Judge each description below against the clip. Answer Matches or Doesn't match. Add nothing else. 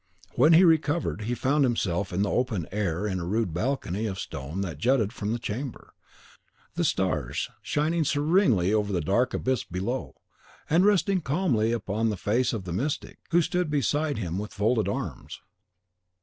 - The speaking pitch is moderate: Doesn't match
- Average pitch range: Doesn't match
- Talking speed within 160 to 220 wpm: Matches